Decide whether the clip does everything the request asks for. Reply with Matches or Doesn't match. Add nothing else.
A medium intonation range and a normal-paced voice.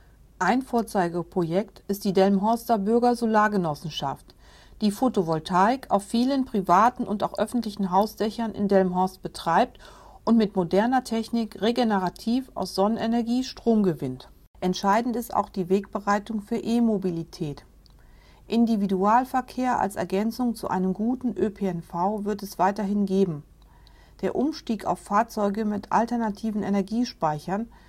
Doesn't match